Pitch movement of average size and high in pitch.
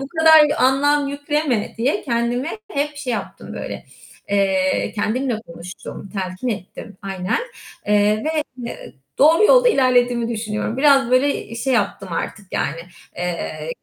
No: wide, 5.9 semitones; high, 235 Hz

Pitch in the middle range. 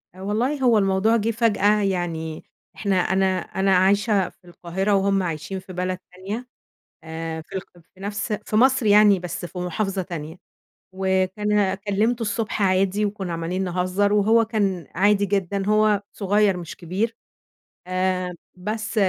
No: high, 195 Hz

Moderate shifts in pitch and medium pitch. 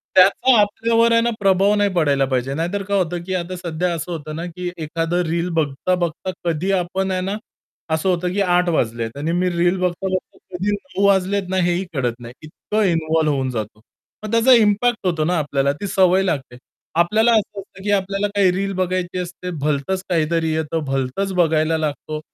Yes: average, 3.6 semitones; medium, 180 Hz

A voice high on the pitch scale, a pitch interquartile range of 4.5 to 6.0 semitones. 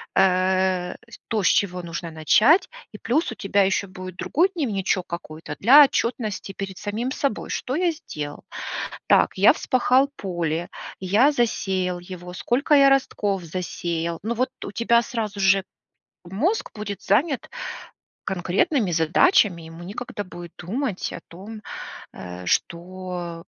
Yes: high, 195 Hz; average, 5.1 semitones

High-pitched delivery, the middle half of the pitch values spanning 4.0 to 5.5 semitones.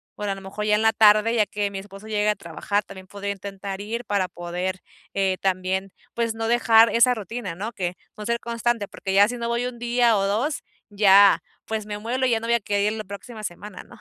No: high, 210 Hz; average, 2.8 semitones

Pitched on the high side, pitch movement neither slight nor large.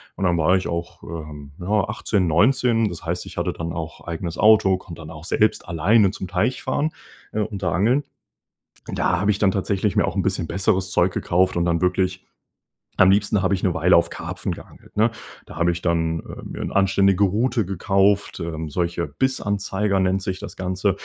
No: very low, 95 Hz; average, 3.0 semitones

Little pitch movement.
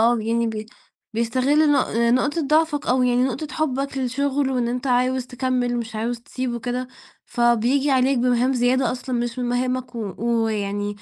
Yes: narrow, 1.9 semitones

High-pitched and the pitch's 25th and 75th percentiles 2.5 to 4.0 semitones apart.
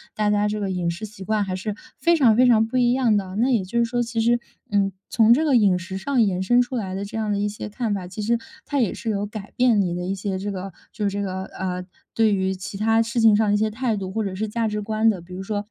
Yes: high, 210 Hz; average, 2.9 semitones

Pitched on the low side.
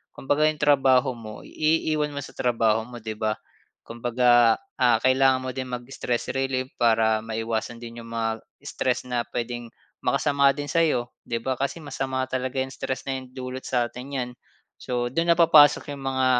Yes: low, 130 Hz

